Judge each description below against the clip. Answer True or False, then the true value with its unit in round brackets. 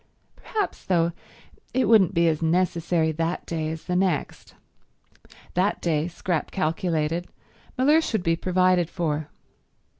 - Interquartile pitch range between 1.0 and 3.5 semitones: True (2.4 semitones)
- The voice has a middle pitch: True (170 Hz)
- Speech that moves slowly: True (125 wpm)